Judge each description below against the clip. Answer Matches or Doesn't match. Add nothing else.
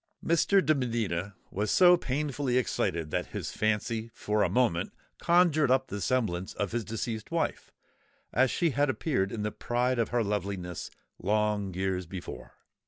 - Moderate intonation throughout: Matches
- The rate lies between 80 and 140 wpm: Doesn't match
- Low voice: Matches